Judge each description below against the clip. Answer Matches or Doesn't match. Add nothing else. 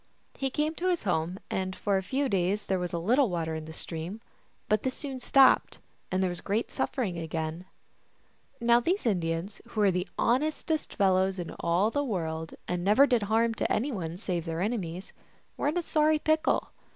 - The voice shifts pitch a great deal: Matches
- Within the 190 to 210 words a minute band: Matches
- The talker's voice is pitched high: Matches